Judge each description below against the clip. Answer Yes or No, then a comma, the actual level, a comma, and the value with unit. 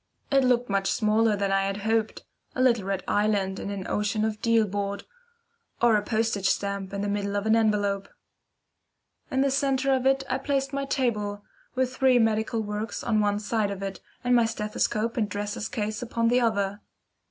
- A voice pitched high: Yes, high, 215 Hz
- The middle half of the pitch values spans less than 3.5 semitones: Yes, average, 2.9 semitones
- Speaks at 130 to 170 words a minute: No, average, 190 wpm